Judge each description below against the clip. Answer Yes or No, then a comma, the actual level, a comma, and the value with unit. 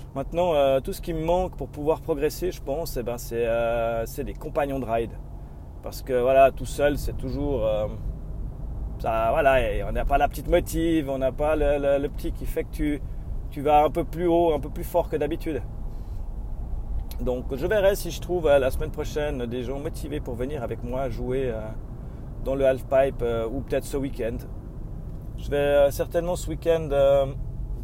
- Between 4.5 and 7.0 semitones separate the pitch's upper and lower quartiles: No, average, 4.1 semitones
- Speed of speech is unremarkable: Yes, average, 205 wpm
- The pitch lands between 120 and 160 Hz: Yes, low, 135 Hz